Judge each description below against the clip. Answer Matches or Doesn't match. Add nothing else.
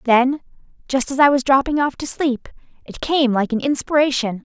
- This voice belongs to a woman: Matches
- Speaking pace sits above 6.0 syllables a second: Doesn't match